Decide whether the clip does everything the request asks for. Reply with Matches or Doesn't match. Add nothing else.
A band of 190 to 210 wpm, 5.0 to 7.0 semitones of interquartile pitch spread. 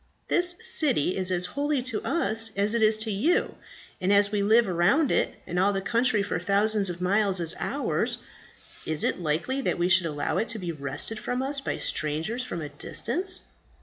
Matches